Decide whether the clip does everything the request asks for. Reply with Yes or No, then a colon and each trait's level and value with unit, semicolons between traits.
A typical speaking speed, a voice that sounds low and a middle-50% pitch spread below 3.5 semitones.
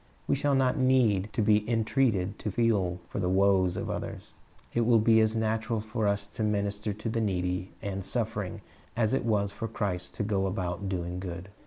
Yes: average, 195 wpm; low, 105 Hz; average, 2.9 semitones